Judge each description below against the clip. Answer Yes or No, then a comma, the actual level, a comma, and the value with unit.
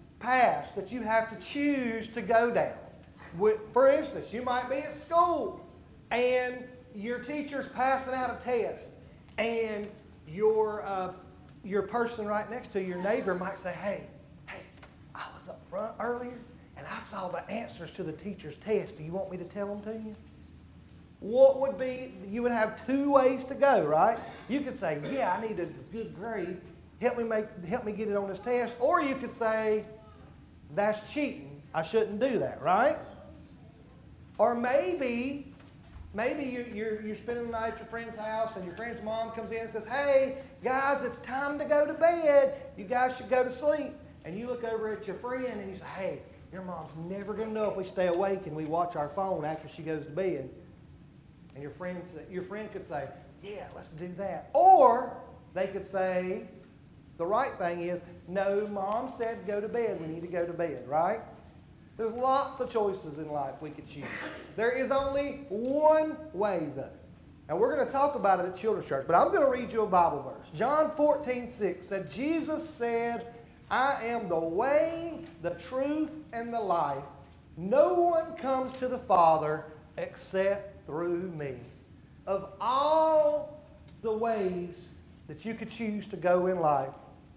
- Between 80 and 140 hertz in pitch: No, high, 220 Hz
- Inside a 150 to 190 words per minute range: Yes, average, 185 wpm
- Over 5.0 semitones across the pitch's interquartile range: Yes, wide, 5.6 semitones